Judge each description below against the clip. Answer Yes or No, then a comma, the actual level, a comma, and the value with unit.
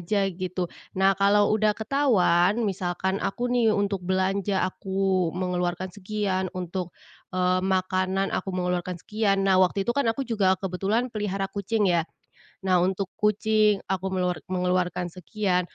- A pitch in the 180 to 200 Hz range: Yes, high, 190 Hz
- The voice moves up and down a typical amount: No, narrow, 2.2 semitones